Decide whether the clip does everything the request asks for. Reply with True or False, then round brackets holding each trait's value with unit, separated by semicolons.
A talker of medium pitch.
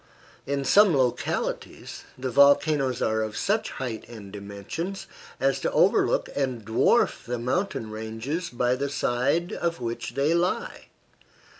False (130 Hz)